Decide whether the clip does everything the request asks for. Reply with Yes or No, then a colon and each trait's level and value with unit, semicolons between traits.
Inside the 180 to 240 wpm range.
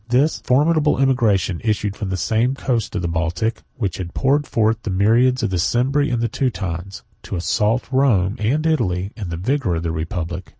Yes: average, 185 wpm